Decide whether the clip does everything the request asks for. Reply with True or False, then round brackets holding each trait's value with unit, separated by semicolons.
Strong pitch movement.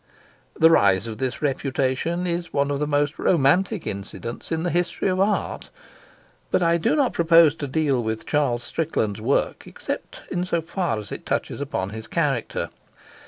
True (6.0 semitones)